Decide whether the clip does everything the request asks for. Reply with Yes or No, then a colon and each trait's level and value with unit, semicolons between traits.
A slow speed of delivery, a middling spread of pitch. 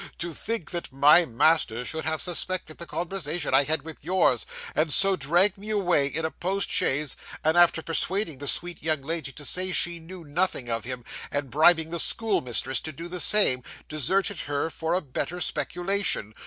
No: average, 190 wpm; average, 4.0 semitones